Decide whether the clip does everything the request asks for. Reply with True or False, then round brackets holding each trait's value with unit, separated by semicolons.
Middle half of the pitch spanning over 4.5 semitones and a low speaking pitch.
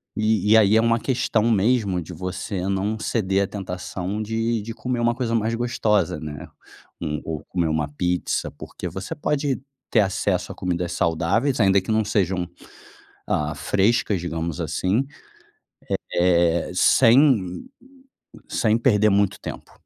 False (4.2 semitones; 100 Hz)